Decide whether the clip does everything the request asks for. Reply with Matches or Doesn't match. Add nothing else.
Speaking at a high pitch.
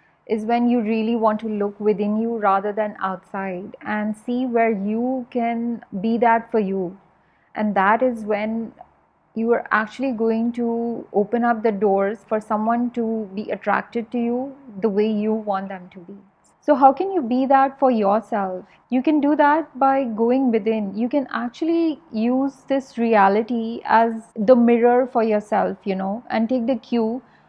Matches